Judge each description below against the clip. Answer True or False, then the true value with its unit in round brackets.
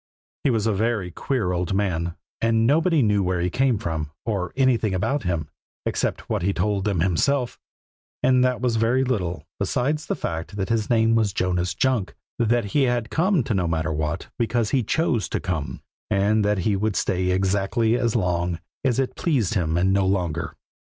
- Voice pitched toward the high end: False (105 Hz)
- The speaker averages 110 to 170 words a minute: False (185 wpm)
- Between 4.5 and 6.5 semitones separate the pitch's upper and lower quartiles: True (5.0 semitones)